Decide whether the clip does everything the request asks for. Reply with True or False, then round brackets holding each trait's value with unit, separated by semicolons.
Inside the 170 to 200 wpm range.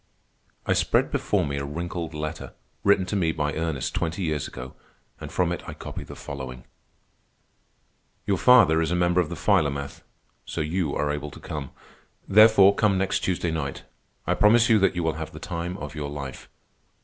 True (185 wpm)